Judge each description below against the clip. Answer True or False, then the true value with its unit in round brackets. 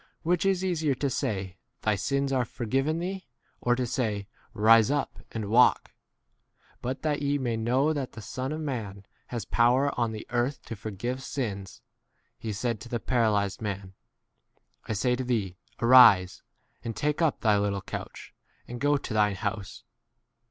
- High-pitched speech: False (120 Hz)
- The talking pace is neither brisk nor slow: True (175 wpm)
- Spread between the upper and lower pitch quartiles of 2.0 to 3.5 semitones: False (4.6 semitones)